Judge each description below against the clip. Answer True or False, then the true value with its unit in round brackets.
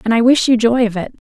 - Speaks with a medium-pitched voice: False (235 Hz)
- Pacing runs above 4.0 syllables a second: True (6.5 syllables/s)